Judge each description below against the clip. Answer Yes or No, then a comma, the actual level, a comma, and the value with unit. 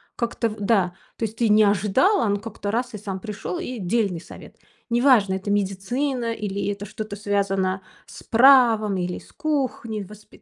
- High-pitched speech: Yes, high, 210 Hz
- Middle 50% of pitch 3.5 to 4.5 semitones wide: No, average, 3.0 semitones